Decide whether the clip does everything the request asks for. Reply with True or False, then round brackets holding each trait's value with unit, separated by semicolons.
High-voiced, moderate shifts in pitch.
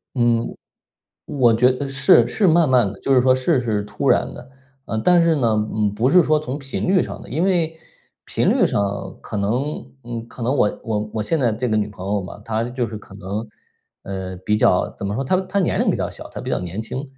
False (120 Hz; 4.8 semitones)